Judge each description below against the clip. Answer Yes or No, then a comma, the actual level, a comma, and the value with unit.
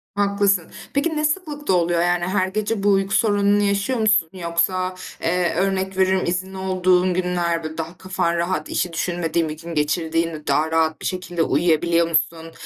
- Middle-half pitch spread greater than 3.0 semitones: No, narrow, 2.6 semitones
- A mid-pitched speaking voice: Yes, medium, 180 Hz